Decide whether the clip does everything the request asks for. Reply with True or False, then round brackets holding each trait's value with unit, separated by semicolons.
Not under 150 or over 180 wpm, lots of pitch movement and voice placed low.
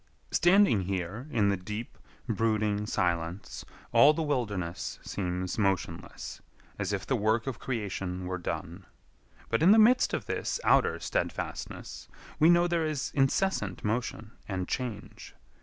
False (140 wpm; 7.0 semitones; 110 Hz)